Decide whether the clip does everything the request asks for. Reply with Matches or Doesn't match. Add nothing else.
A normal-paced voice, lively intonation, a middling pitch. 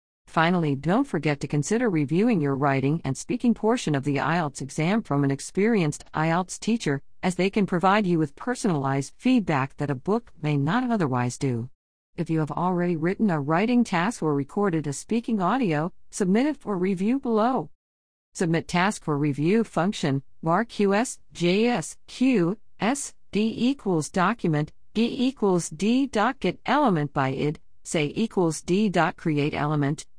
Matches